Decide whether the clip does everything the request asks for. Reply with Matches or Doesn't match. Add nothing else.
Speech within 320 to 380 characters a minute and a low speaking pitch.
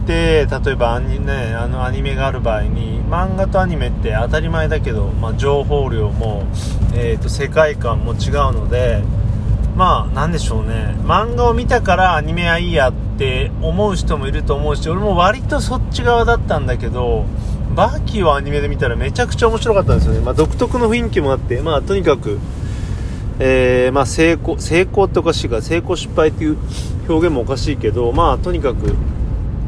Matches